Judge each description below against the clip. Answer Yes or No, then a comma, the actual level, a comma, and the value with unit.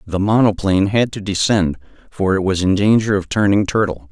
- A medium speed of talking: Yes, average, 190 wpm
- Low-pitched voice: Yes, low, 100 Hz